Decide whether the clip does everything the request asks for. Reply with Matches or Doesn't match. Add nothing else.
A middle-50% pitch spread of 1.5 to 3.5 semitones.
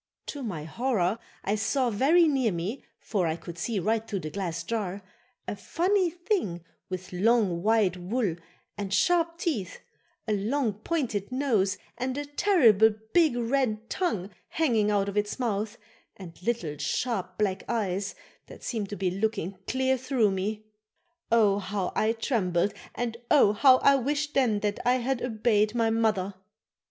Doesn't match